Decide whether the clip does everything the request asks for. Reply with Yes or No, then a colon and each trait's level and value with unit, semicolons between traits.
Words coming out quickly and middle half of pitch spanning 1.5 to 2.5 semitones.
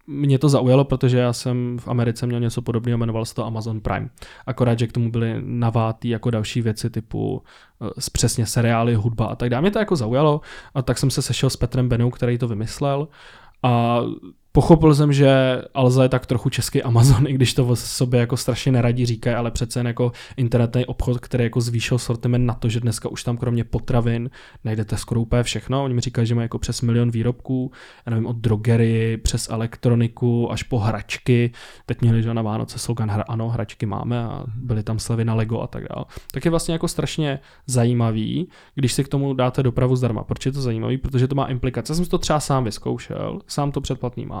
Yes: fast, 210 wpm; narrow, 2.1 semitones